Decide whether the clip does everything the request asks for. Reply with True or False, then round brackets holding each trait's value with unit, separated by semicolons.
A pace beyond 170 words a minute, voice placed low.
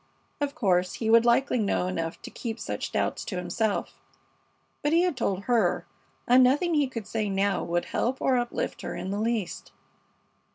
False (180 wpm; 225 Hz)